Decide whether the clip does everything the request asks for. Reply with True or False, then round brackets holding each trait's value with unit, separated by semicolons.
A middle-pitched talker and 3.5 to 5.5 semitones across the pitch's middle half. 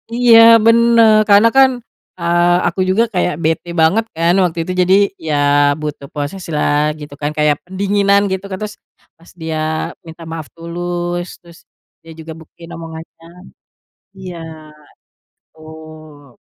False (170 Hz; 3.1 semitones)